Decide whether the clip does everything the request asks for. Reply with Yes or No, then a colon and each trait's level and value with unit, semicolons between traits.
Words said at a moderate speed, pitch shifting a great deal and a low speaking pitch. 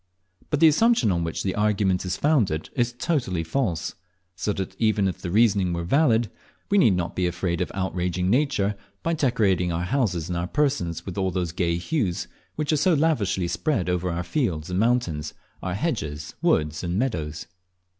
Yes: average, 185 wpm; wide, 6.2 semitones; very low, 95 Hz